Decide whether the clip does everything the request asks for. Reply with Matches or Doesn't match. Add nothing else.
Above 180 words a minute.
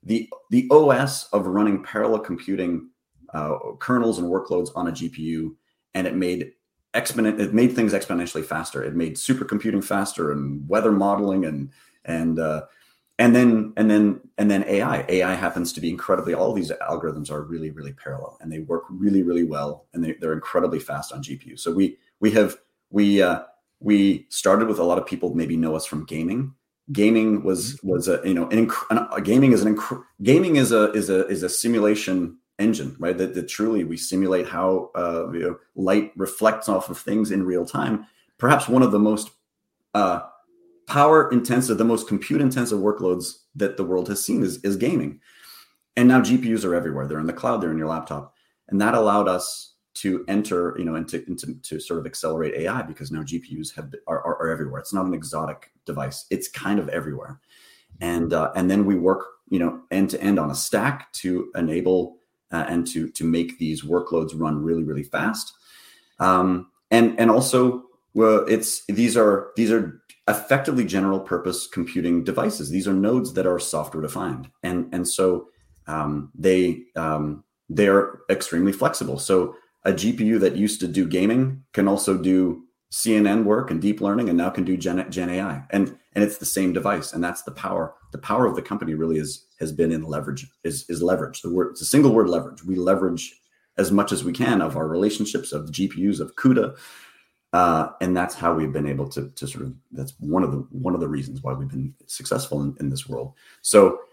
Matches